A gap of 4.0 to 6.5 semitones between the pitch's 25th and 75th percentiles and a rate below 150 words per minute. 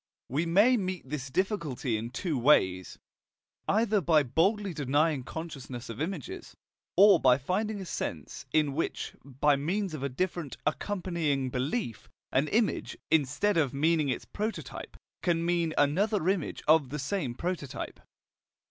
Yes: wide, 5.6 semitones; average, 140 wpm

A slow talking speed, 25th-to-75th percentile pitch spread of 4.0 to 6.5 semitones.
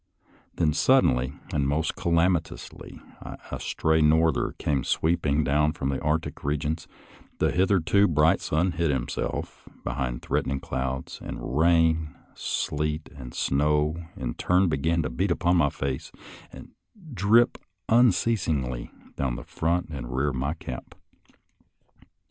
No: slow, 130 wpm; average, 3.6 semitones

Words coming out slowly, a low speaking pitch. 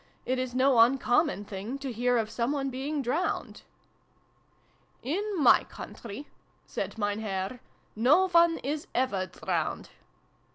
No: slow, 130 wpm; very high, 255 Hz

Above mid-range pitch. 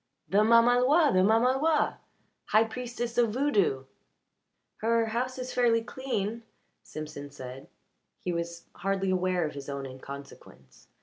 Yes: high, 215 Hz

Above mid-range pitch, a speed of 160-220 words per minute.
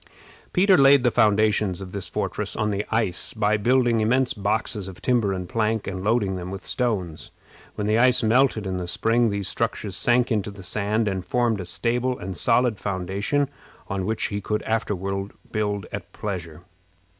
No: low, 105 Hz; average, 180 wpm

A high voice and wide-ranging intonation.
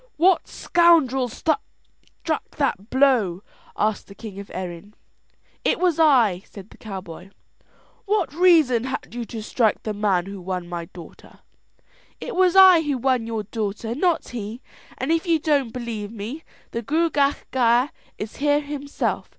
Yes: high, 245 Hz; wide, 6.3 semitones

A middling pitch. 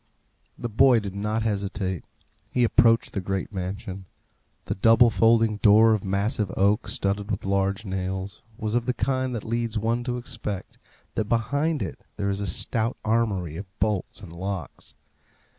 No: low, 105 Hz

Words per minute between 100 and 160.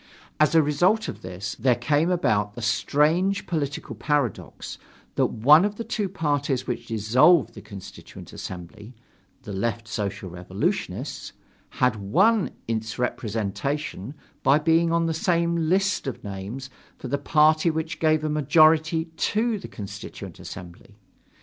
Yes: average, 140 wpm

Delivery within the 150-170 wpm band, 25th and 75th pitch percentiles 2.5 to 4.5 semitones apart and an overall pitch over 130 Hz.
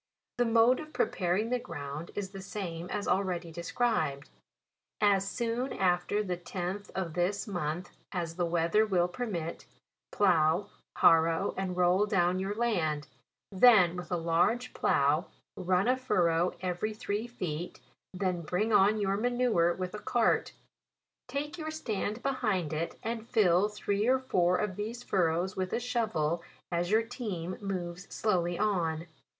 Yes: average, 155 wpm; average, 3.9 semitones; high, 190 Hz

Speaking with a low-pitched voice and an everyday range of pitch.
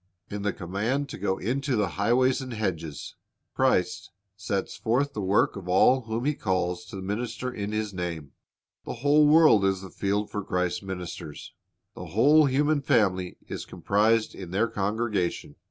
Yes: low, 105 Hz; average, 4.8 semitones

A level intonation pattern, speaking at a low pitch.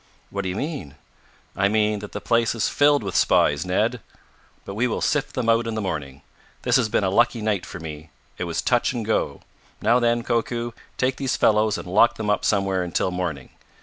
No: average, 4.2 semitones; low, 105 Hz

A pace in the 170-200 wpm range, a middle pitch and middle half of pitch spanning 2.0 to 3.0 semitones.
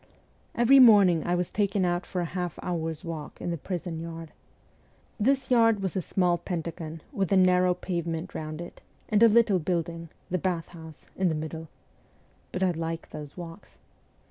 Yes: average, 175 wpm; medium, 175 Hz; narrow, 2.5 semitones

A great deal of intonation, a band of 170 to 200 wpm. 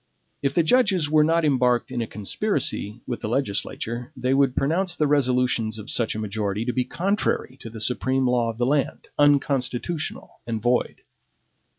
No: average, 4.1 semitones; average, 175 wpm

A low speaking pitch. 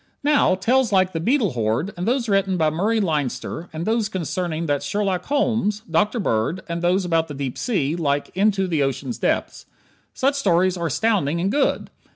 No: medium, 185 Hz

